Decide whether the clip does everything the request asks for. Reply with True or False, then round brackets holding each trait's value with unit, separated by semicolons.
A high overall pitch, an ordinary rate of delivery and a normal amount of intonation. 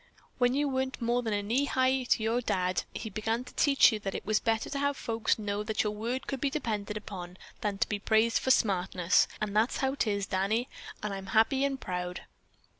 False (220 Hz; 215 wpm; 4.1 semitones)